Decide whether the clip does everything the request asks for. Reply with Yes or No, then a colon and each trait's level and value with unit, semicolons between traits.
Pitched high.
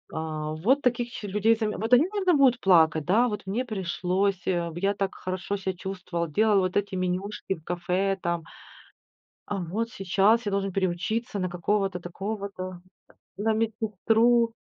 Yes: high, 195 Hz